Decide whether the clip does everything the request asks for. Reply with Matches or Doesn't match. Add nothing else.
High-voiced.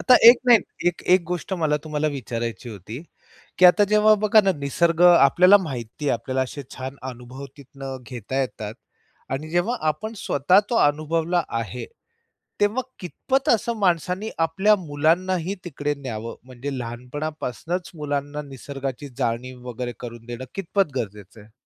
Doesn't match